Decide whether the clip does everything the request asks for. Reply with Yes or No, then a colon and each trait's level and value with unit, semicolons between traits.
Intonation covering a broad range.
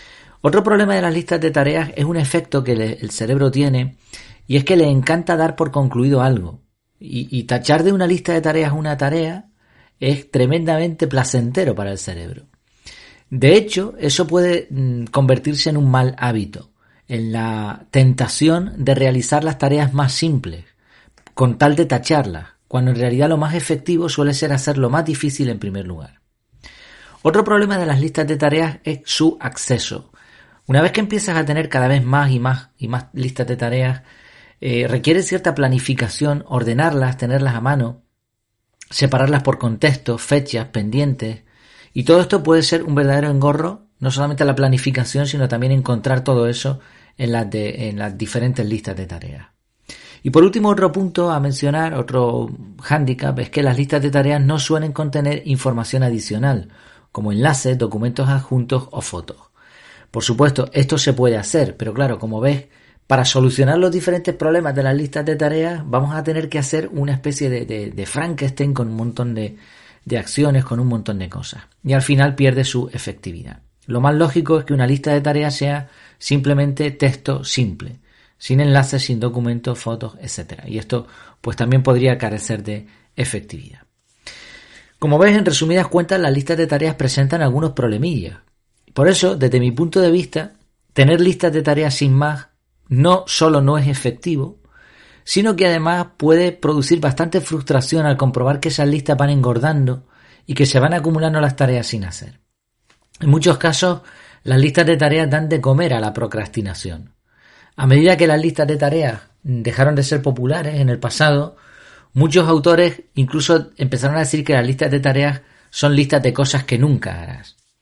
No: average, 4.0 semitones